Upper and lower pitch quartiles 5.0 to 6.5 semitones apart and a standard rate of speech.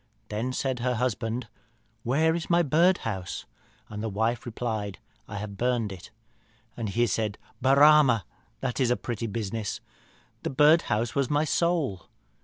No: average, 4.4 semitones; average, 145 wpm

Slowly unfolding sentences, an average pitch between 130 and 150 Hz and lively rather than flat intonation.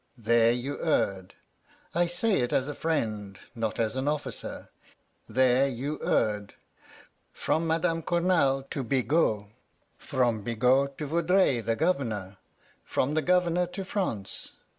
Yes: slow, 130 wpm; low, 135 Hz; wide, 6.3 semitones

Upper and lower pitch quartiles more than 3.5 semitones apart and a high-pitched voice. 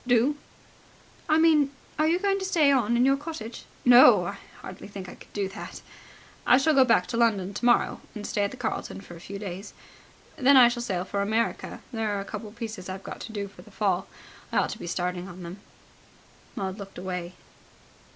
Yes: average, 4.8 semitones; high, 220 Hz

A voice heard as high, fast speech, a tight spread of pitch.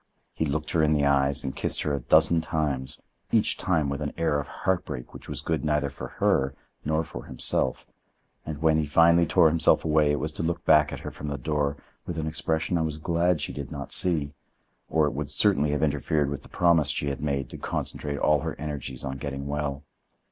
No: very low, 75 Hz; fast, 220 wpm; narrow, 2.1 semitones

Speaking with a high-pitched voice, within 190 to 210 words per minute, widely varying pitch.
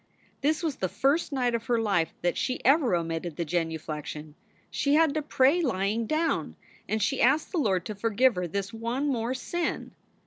Yes: high, 230 Hz; average, 195 wpm; wide, 7.6 semitones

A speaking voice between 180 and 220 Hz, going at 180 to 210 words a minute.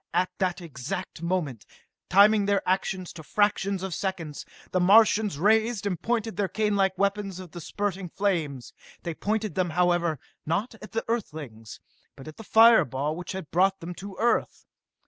No: medium, 185 Hz; average, 165 wpm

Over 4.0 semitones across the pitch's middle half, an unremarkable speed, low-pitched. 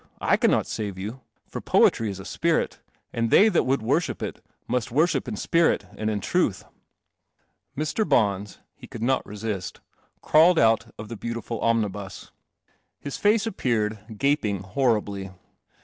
Yes: average, 4.9 semitones; average, 155 wpm; low, 115 Hz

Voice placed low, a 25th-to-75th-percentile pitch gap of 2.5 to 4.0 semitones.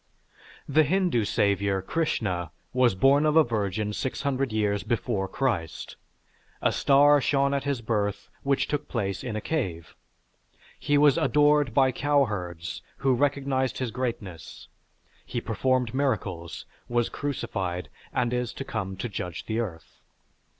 No: low, 120 Hz; wide, 5.5 semitones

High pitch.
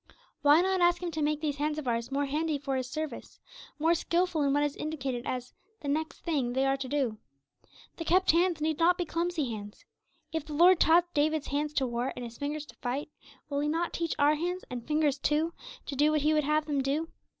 Yes: very high, 300 Hz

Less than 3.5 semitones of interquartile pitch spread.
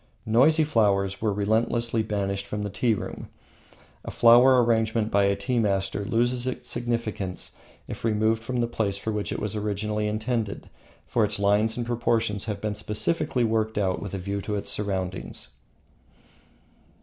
Yes: narrow, 2.6 semitones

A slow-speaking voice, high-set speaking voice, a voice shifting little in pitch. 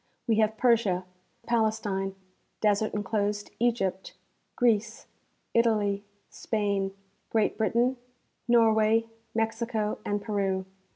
Yes: slow, 95 wpm; high, 215 Hz; narrow, 2.0 semitones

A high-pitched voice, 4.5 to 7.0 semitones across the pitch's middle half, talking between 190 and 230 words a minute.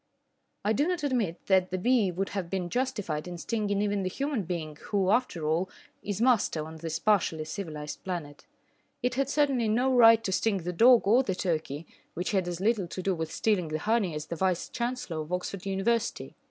Yes: high, 195 Hz; average, 5.2 semitones; fast, 205 wpm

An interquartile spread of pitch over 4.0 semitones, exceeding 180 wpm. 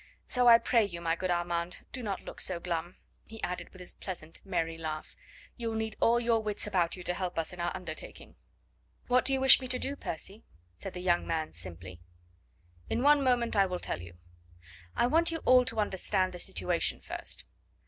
Yes: wide, 5.4 semitones; fast, 205 wpm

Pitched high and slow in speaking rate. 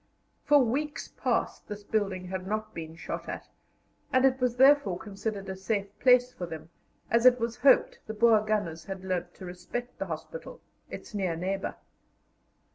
No: high, 210 Hz; average, 170 wpm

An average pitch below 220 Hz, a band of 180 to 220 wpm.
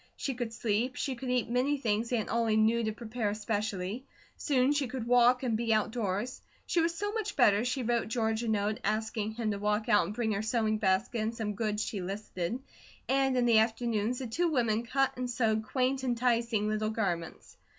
No: high, 230 Hz; average, 200 wpm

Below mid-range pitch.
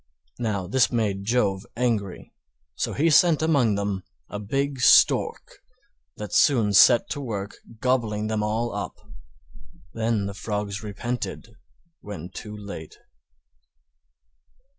Yes: low, 110 Hz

